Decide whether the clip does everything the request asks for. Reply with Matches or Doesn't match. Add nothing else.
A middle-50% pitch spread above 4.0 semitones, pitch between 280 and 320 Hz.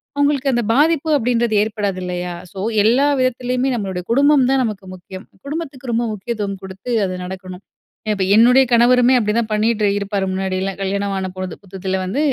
Doesn't match